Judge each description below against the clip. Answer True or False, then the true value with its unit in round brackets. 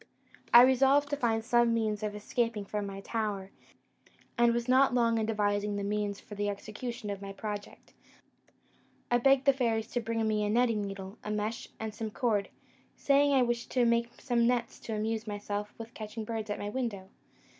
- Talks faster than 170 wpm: True (190 wpm)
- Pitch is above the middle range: True (225 Hz)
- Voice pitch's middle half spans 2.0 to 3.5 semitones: True (2.4 semitones)